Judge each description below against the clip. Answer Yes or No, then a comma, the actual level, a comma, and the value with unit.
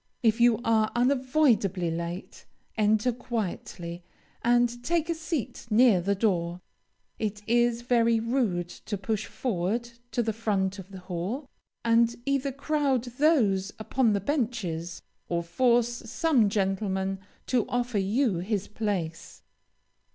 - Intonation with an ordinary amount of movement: Yes, average, 4.1 semitones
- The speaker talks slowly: Yes, slow, 130 wpm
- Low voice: No, high, 220 Hz